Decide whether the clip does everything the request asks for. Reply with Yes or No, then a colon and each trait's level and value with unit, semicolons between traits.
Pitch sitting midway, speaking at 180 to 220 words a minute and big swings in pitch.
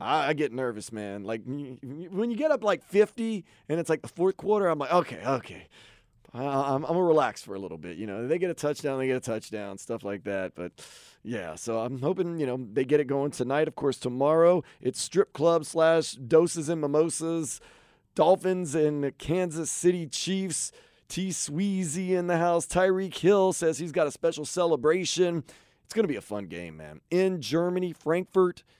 Yes: medium, 155 Hz; average, 195 wpm; wide, 6.0 semitones